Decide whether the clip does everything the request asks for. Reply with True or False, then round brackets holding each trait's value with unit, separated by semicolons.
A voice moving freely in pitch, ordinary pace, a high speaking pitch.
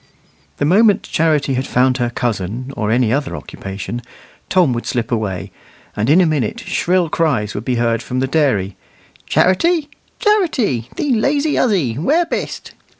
False (8.0 semitones; 155 wpm; 135 Hz)